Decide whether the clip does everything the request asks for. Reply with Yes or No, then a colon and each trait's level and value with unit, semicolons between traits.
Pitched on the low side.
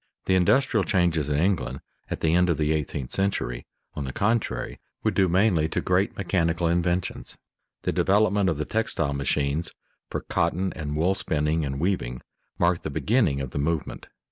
Yes: very low, 85 Hz